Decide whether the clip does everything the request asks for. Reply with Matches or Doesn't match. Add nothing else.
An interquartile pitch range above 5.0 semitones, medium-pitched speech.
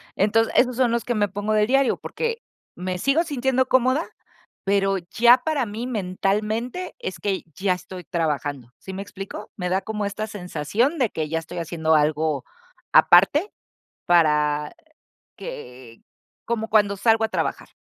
Doesn't match